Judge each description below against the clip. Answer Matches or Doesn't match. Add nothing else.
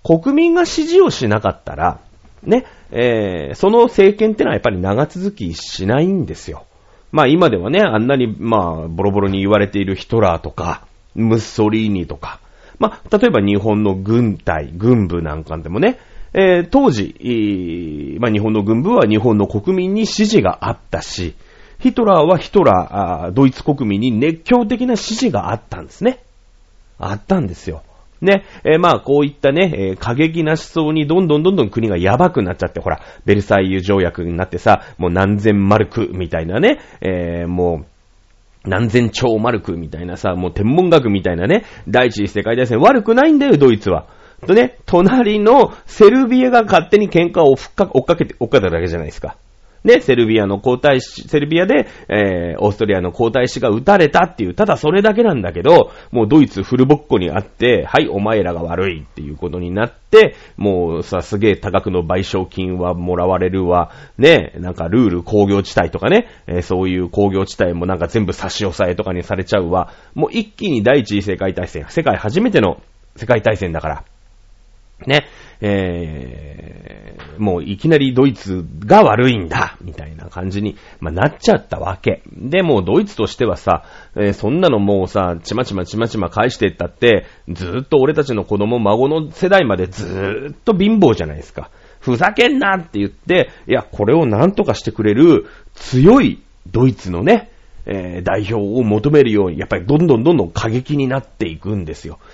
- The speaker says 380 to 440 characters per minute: Doesn't match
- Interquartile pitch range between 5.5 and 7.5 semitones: Doesn't match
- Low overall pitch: Matches